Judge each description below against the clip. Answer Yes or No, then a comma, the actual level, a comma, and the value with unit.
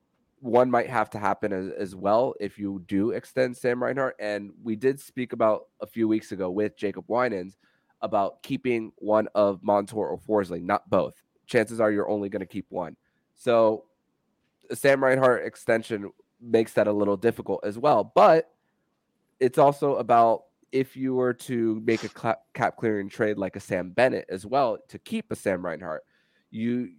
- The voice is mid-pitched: No, low, 110 Hz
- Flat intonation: No, average, 3.1 semitones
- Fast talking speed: No, average, 175 wpm